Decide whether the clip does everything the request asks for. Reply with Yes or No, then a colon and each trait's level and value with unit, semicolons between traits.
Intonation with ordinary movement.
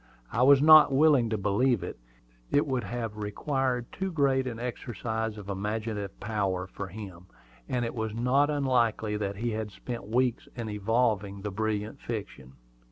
Yes: average, 3.4 semitones